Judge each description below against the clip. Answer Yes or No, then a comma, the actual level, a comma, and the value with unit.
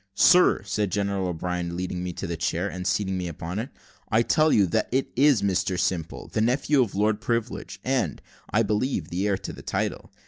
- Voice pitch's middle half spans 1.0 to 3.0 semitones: No, average, 4.3 semitones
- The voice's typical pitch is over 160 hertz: No, low, 100 Hz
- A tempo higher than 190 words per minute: Yes, average, 200 wpm